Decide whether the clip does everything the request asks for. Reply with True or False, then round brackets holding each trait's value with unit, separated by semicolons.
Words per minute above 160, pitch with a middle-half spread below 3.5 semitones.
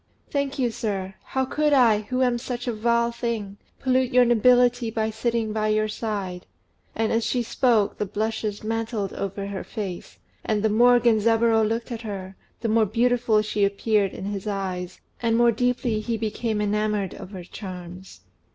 True (180 wpm; 2.5 semitones)